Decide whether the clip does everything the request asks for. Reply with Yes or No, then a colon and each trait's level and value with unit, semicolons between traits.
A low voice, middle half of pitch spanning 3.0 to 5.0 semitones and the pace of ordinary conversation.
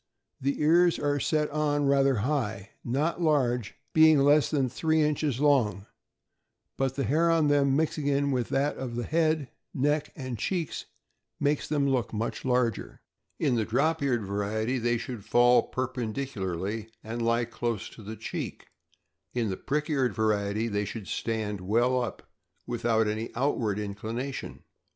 Yes: low, 125 Hz; average, 4.6 semitones; average, 155 wpm